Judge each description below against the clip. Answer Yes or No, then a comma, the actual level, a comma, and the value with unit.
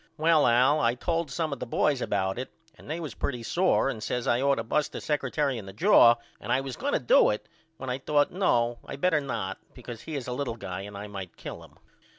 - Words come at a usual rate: No, fast, 245 wpm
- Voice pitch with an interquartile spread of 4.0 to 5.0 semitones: Yes, average, 4.3 semitones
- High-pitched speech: No, low, 125 Hz